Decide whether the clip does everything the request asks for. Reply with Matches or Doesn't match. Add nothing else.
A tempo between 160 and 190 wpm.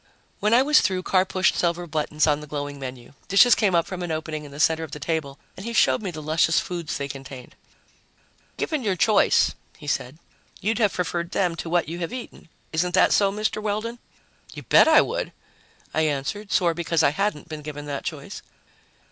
Doesn't match